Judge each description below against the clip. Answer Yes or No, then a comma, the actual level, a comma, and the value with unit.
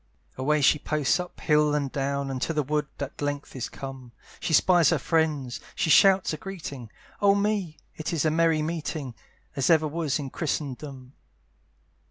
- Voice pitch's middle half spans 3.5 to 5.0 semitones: No, average, 2.9 semitones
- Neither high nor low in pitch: Yes, medium, 150 Hz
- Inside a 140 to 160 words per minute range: No, average, 175 wpm